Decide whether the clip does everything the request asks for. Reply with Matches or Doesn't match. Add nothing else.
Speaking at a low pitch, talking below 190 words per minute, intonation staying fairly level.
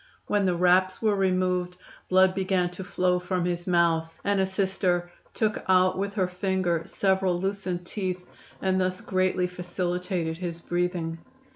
Doesn't match